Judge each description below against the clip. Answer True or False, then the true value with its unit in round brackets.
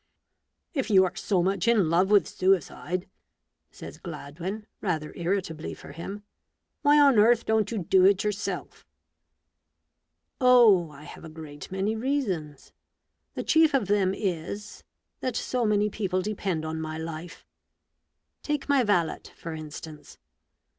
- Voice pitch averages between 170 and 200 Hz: True (190 Hz)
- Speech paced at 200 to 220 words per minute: False (145 wpm)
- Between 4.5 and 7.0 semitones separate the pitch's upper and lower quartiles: True (4.8 semitones)